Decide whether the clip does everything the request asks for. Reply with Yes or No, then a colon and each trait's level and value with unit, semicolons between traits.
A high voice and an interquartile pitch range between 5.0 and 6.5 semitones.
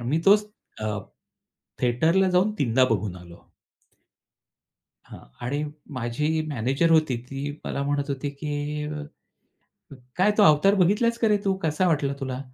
No: medium, 150 Hz; wide, 5.4 semitones